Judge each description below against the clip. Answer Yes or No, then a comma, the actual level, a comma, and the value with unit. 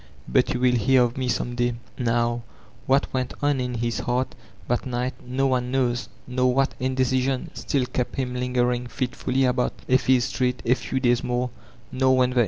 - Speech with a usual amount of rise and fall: No, narrow, 1.1 semitones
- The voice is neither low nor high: No, low, 125 Hz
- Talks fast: No, average, 185 wpm